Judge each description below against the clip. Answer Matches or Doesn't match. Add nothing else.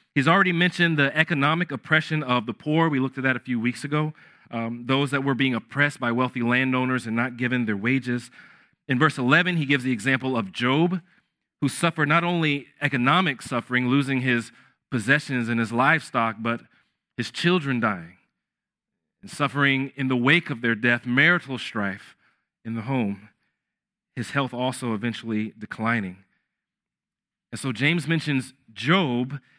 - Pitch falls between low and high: Doesn't match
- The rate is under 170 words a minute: Matches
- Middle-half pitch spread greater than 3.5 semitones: Matches